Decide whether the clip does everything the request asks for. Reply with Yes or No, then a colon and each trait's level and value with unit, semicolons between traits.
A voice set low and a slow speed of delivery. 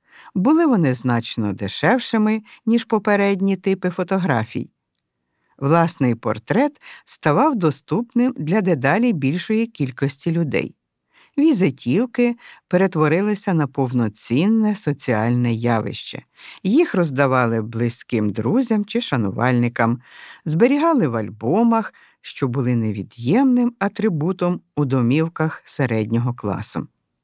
No: medium, 155 Hz; slow, 90 wpm